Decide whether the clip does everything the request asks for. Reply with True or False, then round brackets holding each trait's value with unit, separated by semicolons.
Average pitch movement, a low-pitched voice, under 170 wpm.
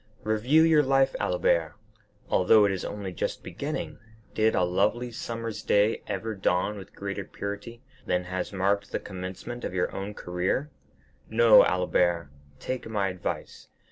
True (3.8 semitones; 100 Hz; 140 wpm)